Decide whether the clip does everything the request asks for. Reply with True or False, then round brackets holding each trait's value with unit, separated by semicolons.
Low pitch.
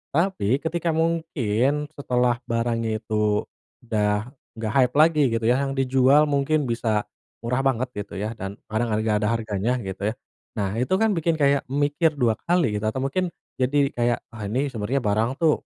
True (125 Hz)